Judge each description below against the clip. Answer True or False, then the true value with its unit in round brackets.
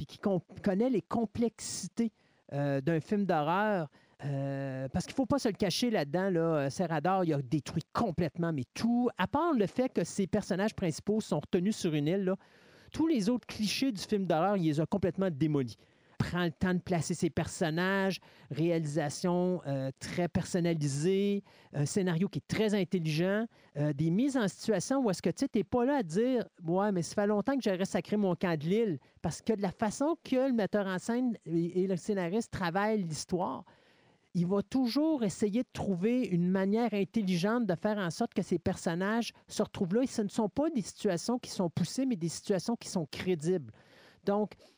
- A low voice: False (190 Hz)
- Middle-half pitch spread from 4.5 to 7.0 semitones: False (4.1 semitones)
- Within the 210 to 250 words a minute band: False (200 wpm)